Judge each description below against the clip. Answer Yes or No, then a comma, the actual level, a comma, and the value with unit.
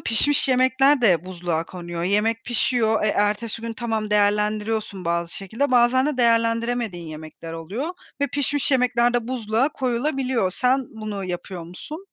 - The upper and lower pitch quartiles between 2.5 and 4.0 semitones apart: No, average, 4.5 semitones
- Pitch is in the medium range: No, high, 225 Hz